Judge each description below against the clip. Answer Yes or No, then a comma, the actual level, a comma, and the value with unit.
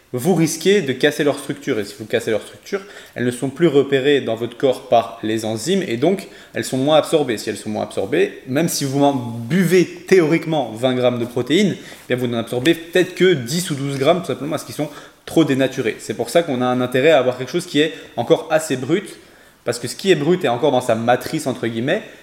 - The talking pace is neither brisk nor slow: No, fast, 245 wpm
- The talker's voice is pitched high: No, medium, 140 Hz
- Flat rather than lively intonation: No, average, 4.8 semitones